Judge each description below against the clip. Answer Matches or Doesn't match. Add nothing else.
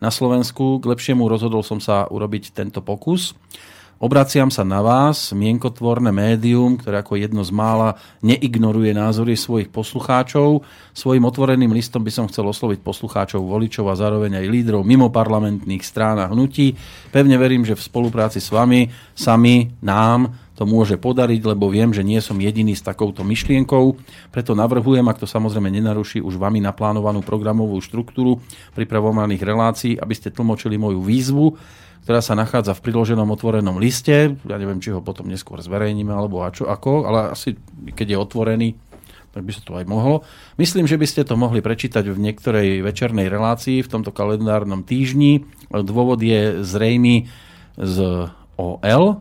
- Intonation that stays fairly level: Doesn't match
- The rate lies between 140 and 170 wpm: Matches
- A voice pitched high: Doesn't match